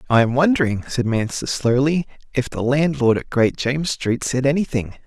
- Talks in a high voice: No, low, 130 Hz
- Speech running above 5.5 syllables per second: No, 5.2 syllables/s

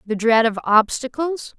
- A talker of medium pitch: No, high, 240 Hz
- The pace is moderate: Yes, average, 150 wpm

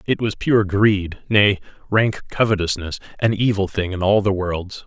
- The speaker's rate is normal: Yes, average, 175 wpm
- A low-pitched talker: Yes, low, 100 Hz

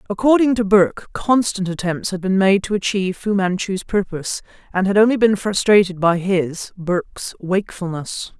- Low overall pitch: No, high, 195 Hz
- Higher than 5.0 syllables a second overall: Yes, 5.5 syllables/s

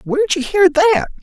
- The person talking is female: No, male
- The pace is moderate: Yes, average, 195 wpm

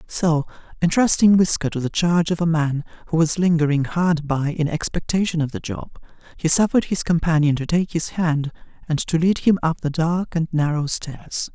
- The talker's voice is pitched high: No, medium, 160 Hz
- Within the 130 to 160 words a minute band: No, average, 190 wpm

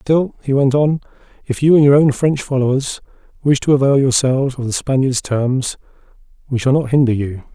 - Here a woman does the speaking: No, male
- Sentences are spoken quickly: No, average, 190 wpm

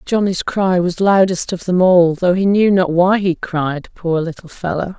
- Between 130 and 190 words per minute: No, fast, 205 wpm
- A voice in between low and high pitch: Yes, medium, 180 Hz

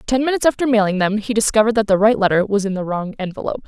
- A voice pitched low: No, high, 215 Hz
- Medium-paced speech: No, fast, 260 wpm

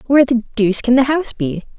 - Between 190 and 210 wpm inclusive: No, fast, 235 wpm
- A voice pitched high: Yes, high, 240 Hz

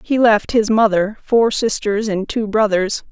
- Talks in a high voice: Yes, high, 215 Hz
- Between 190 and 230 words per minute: No, average, 175 wpm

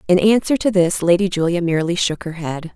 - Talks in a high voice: No, medium, 180 Hz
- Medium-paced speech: No, fast, 220 wpm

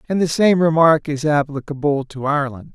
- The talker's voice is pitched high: No, medium, 150 Hz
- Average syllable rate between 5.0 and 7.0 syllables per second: Yes, 5.5 syllables/s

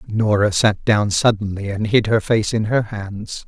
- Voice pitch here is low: Yes, low, 105 Hz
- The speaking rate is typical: Yes, average, 190 wpm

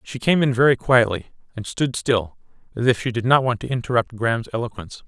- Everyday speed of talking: No, fast, 215 wpm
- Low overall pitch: Yes, low, 120 Hz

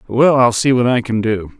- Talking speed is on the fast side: Yes, fast, 265 wpm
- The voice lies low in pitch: Yes, low, 120 Hz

